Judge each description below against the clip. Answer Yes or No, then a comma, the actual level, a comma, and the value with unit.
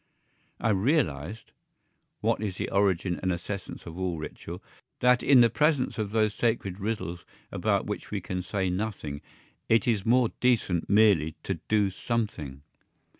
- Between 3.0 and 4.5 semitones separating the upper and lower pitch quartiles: Yes, average, 4.1 semitones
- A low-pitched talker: Yes, low, 100 Hz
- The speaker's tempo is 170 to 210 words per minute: No, average, 150 wpm